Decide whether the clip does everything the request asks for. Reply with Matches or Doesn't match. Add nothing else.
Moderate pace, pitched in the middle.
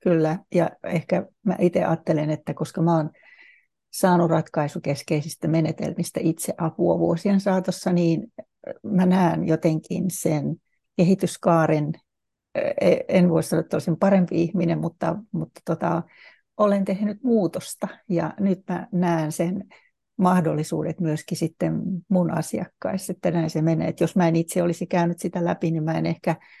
Matches